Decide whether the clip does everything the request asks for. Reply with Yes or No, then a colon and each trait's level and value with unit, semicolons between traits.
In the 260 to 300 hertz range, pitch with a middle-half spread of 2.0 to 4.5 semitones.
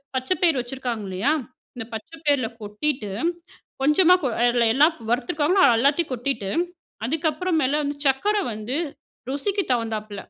No: very high, 270 Hz; average, 4.9 semitones